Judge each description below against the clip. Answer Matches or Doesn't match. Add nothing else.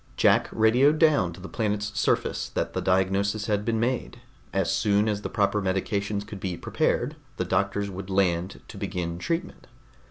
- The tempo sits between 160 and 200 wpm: Matches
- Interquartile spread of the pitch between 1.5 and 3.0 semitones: Matches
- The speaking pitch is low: Matches